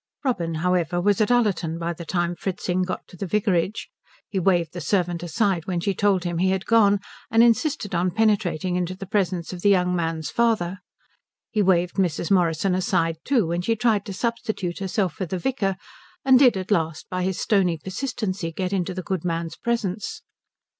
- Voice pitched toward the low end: No, medium, 185 Hz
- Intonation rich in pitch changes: No, average, 3.0 semitones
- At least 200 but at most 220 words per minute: No, average, 190 wpm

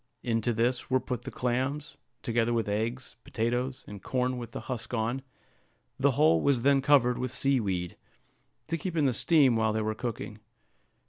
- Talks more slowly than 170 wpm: No, average, 180 wpm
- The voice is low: Yes, low, 120 Hz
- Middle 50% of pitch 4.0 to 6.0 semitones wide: No, average, 2.7 semitones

